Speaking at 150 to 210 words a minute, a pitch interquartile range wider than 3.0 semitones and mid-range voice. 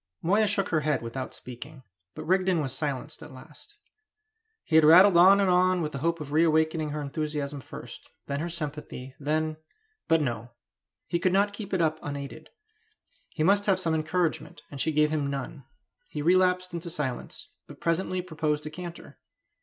Yes: average, 175 wpm; average, 3.6 semitones; medium, 155 Hz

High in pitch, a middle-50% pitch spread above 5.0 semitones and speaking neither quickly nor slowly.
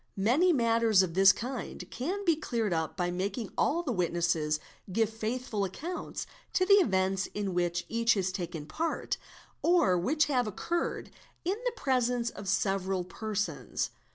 Yes: high, 215 Hz; wide, 5.5 semitones; average, 155 wpm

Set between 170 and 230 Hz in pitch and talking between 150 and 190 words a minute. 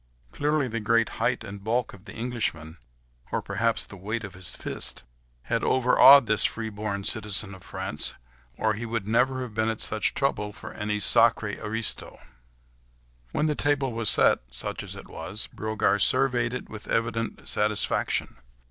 No: low, 110 Hz; average, 160 wpm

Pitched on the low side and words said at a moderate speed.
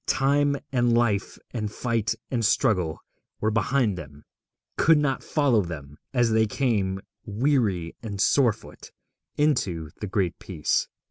No: low, 110 Hz; slow, 130 wpm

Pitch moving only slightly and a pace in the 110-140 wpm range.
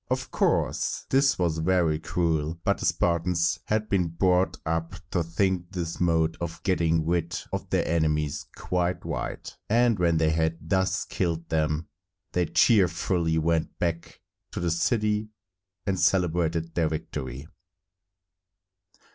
Yes: narrow, 2.2 semitones; slow, 135 wpm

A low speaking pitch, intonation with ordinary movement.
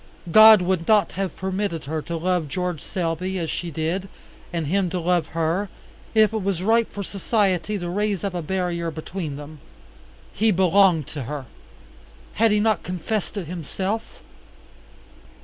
No: medium, 180 Hz; average, 3.4 semitones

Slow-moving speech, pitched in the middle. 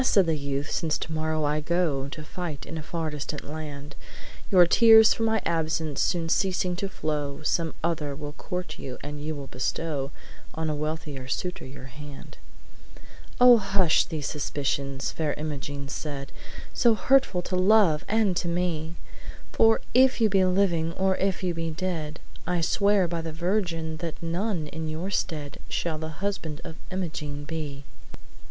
No: average, 165 wpm; medium, 160 Hz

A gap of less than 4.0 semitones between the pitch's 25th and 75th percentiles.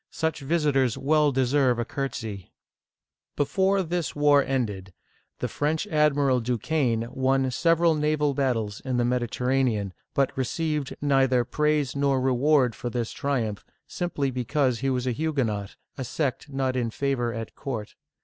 Yes: average, 3.3 semitones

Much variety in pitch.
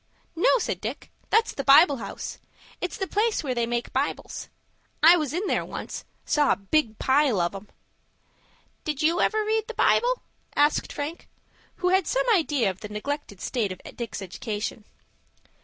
Yes: wide, 8.3 semitones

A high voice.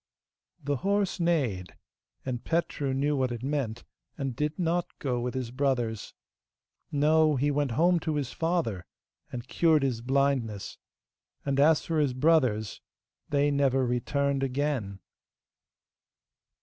No: medium, 140 Hz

